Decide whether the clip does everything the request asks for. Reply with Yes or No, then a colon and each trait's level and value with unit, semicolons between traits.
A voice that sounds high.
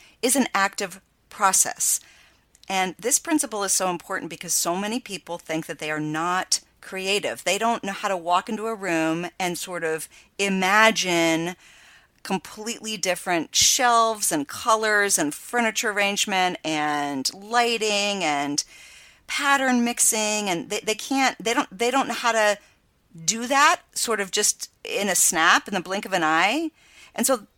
Yes: high, 200 Hz